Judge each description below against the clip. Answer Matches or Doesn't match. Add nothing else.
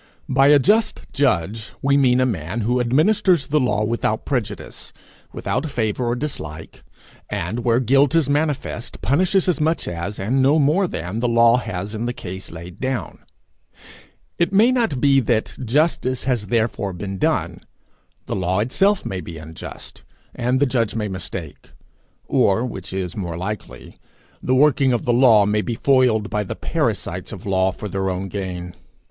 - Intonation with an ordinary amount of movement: Doesn't match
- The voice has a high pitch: Doesn't match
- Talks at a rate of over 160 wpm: Matches